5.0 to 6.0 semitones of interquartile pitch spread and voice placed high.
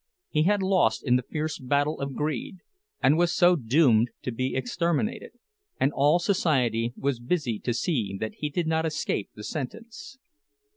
No: wide, 5.4 semitones; medium, 145 Hz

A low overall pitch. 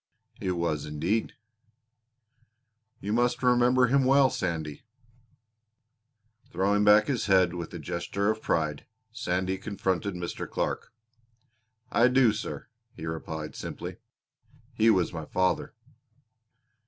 Yes: very low, 95 Hz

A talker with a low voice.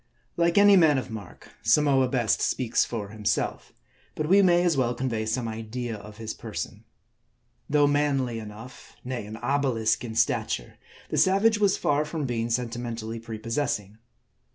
Yes: low, 125 Hz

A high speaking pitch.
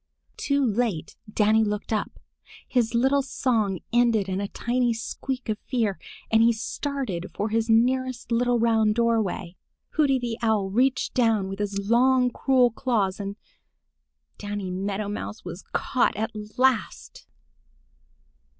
Yes: high, 225 Hz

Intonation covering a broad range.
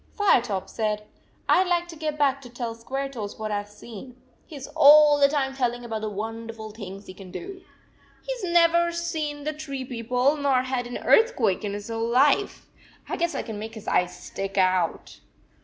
Yes: wide, 5.7 semitones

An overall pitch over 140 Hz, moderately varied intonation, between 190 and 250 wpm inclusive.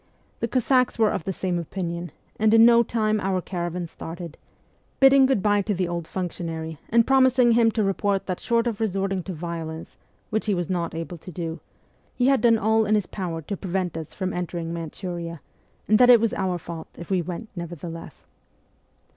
Yes: high, 190 Hz; average, 4.4 semitones; average, 195 wpm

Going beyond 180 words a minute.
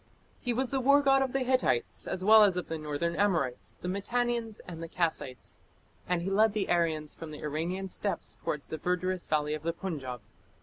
Yes: fast, 205 wpm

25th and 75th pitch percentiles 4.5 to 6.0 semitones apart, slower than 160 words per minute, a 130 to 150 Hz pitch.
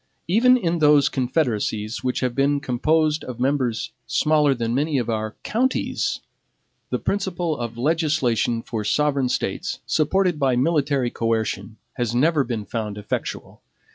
Yes: average, 4.9 semitones; average, 140 wpm; low, 135 Hz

